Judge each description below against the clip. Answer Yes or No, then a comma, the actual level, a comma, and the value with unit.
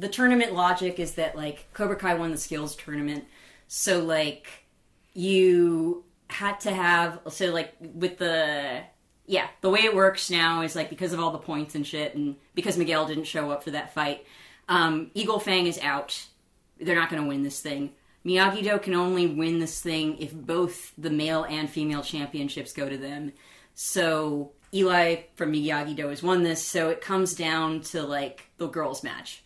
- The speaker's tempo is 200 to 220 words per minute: No, average, 185 wpm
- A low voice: No, medium, 165 Hz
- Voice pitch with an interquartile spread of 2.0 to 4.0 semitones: Yes, average, 3.0 semitones